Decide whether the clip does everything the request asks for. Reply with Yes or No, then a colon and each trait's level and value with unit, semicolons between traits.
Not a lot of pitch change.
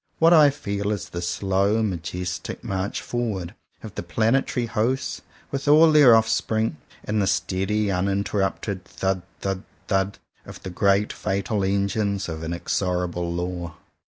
No: average, 3.2 semitones